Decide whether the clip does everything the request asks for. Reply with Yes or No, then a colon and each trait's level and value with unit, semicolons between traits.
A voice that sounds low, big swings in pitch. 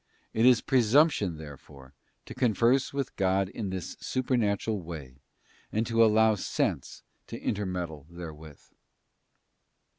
Yes: low, 100 Hz; wide, 6.0 semitones